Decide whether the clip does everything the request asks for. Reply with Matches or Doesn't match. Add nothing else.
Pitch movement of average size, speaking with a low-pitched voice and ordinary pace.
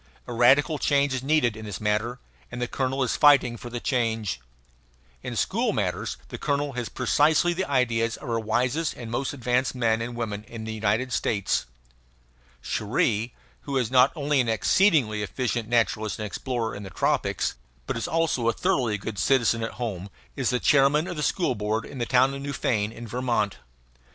Matches